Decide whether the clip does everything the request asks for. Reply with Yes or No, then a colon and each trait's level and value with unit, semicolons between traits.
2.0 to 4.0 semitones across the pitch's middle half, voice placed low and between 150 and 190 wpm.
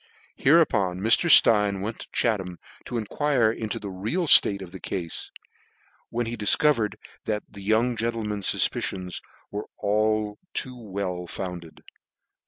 No: average, 3.2 semitones; low, 105 Hz; slow, 135 wpm